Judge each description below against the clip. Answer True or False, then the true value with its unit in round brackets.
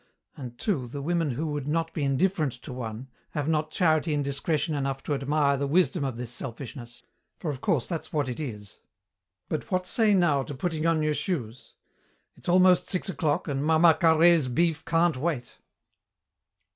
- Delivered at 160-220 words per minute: True (180 wpm)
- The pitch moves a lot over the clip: False (3.7 semitones)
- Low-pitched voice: False (150 Hz)